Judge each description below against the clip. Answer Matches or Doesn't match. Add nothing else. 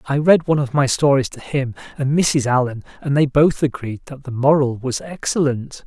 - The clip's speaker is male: Matches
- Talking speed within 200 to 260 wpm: Matches